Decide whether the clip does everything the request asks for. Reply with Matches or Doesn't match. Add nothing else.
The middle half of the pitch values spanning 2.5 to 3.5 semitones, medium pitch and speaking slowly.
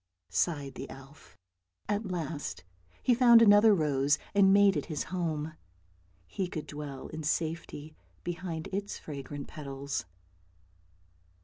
Doesn't match